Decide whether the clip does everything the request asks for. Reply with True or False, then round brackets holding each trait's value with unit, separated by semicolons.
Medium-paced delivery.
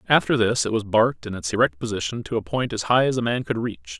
False (285 wpm)